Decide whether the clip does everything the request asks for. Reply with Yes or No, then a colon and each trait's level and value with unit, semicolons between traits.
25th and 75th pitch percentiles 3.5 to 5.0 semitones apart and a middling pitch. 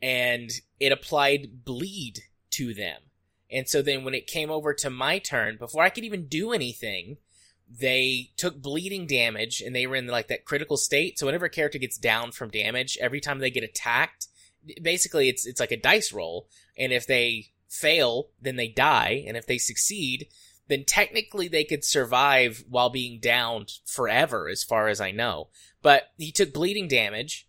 No: average, 4.5 semitones; low, 130 Hz